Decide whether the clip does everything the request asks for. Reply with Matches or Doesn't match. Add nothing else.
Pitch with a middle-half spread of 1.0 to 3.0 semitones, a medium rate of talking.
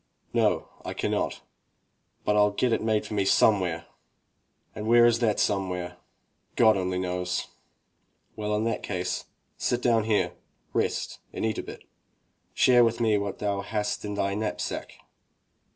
Matches